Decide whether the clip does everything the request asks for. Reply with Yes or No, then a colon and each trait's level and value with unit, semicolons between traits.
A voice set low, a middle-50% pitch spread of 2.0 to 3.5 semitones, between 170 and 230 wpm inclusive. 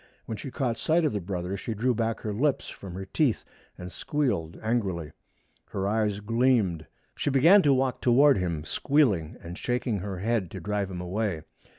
No: low, 105 Hz; wide, 5.6 semitones; average, 185 wpm